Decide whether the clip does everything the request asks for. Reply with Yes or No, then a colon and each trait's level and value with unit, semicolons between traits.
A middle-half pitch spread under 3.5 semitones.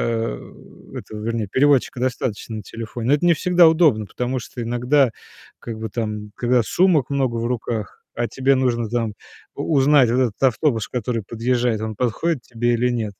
Yes: average, 2.8 semitones